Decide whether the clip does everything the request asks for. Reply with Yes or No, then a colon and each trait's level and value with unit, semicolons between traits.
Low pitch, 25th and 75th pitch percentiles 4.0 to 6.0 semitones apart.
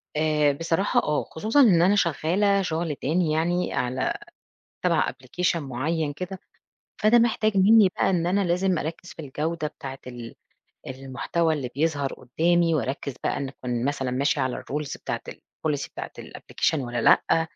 No: medium, 160 Hz; average, 4.6 semitones